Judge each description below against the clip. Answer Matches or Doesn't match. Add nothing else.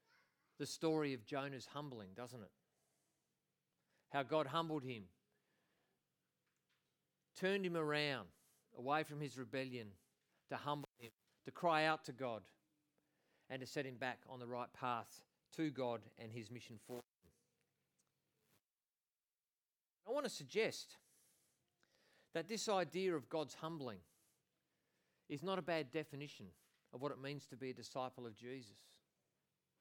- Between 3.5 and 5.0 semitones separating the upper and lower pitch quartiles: Matches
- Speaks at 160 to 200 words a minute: Doesn't match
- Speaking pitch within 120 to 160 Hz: Matches